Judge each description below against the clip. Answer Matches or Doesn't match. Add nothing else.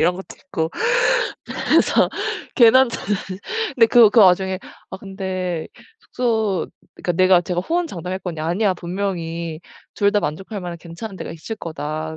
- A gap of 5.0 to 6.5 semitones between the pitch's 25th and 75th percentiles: Doesn't match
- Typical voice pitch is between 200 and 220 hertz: Doesn't match